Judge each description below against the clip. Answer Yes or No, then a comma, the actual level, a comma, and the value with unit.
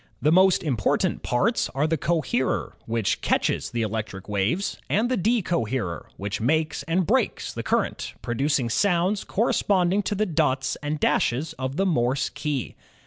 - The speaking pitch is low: No, medium, 150 Hz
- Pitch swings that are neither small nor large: No, wide, 7.4 semitones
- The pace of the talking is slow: No, average, 155 wpm